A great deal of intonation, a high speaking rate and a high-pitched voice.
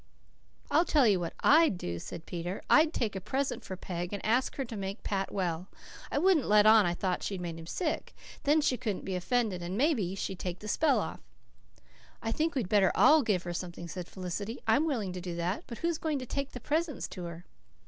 Yes: wide, 7.2 semitones; fast, 225 wpm; high, 205 Hz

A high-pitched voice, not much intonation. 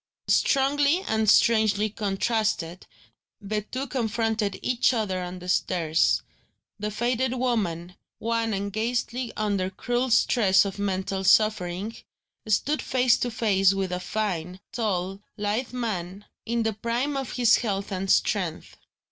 No: high, 215 Hz; average, 3.7 semitones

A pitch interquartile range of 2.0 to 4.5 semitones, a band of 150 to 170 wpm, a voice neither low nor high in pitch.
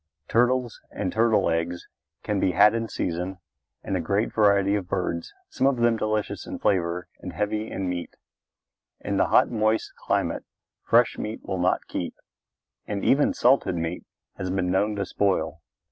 No: average, 3.6 semitones; average, 165 wpm; low, 100 Hz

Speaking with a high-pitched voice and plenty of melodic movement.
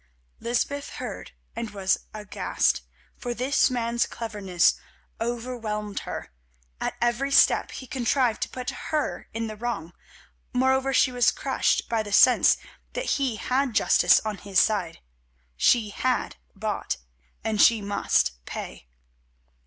No: high, 230 Hz; average, 3.4 semitones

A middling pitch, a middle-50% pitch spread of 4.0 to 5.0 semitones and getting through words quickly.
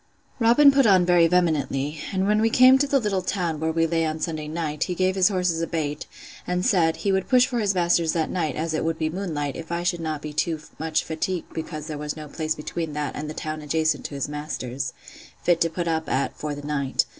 No: medium, 165 Hz; average, 3.0 semitones; fast, 250 wpm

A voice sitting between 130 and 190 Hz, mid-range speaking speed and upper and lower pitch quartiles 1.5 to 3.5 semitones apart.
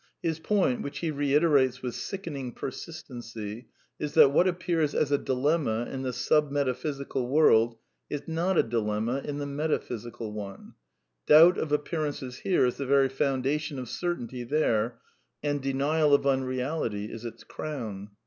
No: medium, 140 Hz; average, 155 wpm; average, 3.9 semitones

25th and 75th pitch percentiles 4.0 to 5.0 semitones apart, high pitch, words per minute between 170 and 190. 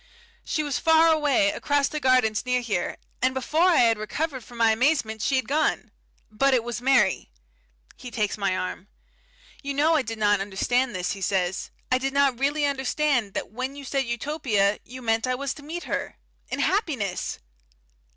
Yes: average, 4.6 semitones; very high, 255 Hz; average, 185 wpm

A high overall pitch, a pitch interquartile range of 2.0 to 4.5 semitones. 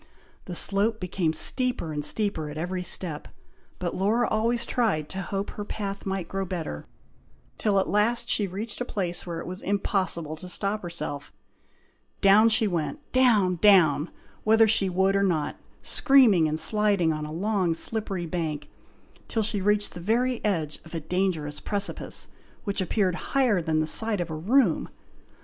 Yes: high, 195 Hz; average, 4.2 semitones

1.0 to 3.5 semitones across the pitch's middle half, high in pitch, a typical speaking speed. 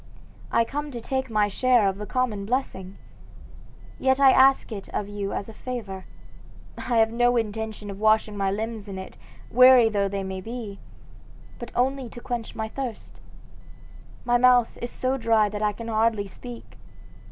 Yes: average, 3.2 semitones; high, 225 Hz; average, 170 wpm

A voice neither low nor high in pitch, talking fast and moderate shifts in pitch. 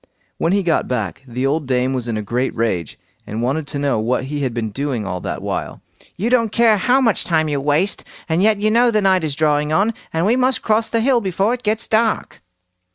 No: medium, 160 Hz; fast, 235 wpm; wide, 9.0 semitones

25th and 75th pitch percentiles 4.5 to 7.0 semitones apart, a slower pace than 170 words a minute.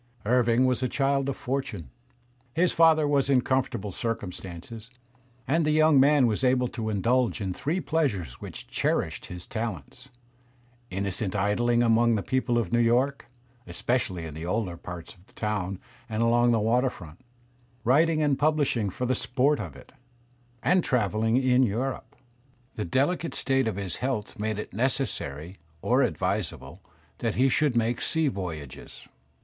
Yes: average, 5.1 semitones; average, 160 wpm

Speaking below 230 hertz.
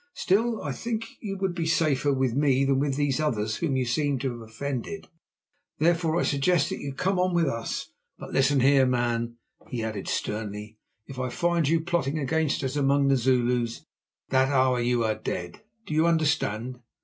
Yes: low, 135 Hz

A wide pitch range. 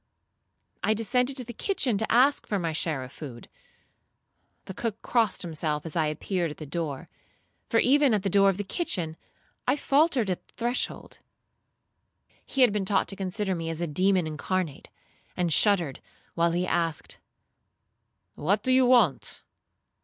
Yes: wide, 6.1 semitones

